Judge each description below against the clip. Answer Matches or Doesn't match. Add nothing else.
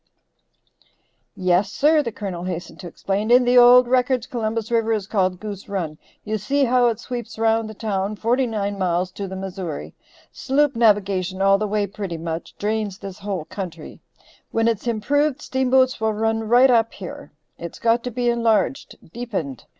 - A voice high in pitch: Matches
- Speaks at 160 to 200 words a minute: Matches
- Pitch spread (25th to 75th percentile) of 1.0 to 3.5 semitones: Doesn't match